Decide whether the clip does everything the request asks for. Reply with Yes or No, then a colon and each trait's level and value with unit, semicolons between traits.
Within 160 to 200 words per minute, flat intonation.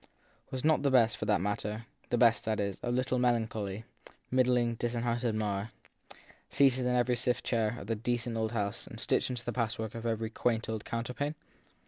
Yes: average, 190 wpm; narrow, 2.0 semitones